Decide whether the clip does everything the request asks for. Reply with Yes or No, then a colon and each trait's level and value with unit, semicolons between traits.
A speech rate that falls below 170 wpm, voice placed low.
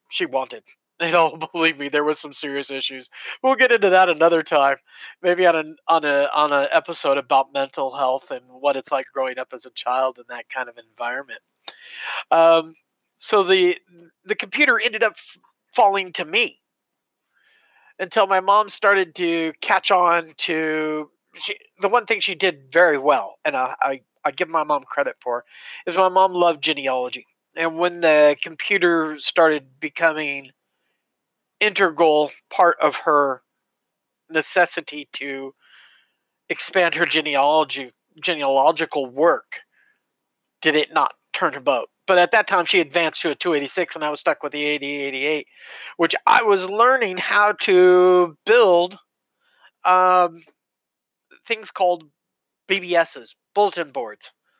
No: average, 150 wpm; medium, 165 Hz